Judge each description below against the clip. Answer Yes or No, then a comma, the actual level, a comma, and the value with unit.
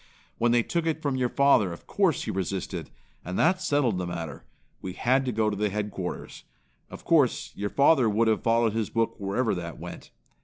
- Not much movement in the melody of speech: No, average, 5.2 semitones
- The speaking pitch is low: Yes, low, 110 Hz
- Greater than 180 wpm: Yes, average, 200 wpm